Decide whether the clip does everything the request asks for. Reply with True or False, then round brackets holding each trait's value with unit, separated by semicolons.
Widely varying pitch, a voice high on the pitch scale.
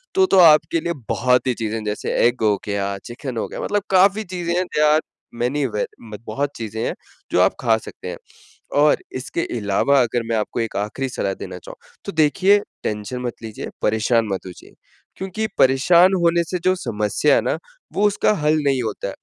False (7.5 semitones; 130 Hz)